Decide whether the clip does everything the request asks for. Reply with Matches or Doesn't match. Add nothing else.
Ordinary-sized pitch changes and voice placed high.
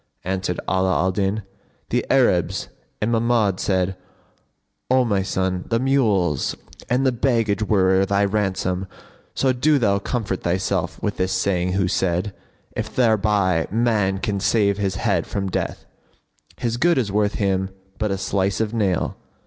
Doesn't match